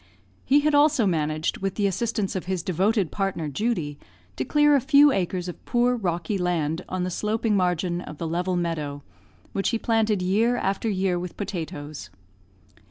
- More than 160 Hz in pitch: Yes, medium, 185 Hz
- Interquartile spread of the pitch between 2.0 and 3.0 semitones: No, average, 4.7 semitones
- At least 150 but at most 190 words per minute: Yes, average, 170 wpm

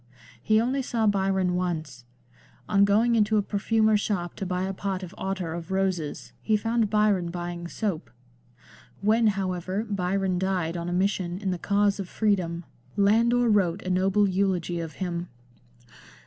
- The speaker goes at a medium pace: Yes, average, 160 wpm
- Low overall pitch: No, high, 190 Hz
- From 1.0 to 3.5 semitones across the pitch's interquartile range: Yes, average, 2.9 semitones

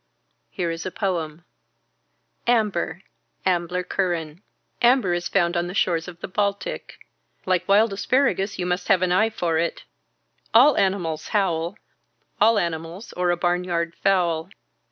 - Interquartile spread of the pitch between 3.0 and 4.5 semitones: No, narrow, 2.6 semitones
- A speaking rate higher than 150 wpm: No, average, 140 wpm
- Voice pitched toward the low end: No, medium, 180 Hz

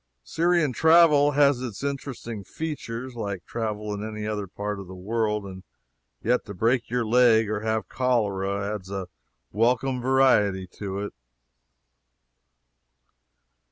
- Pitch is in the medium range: No, low, 110 Hz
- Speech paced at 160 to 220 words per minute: No, slow, 135 wpm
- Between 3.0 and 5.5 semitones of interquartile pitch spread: Yes, average, 4.0 semitones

